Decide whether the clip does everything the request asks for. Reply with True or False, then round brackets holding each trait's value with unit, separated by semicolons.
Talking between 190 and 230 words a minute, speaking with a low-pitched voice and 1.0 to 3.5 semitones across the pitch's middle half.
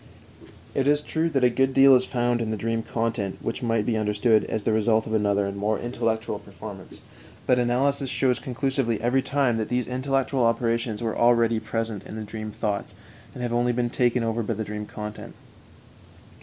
True (195 wpm; 115 Hz; 2.4 semitones)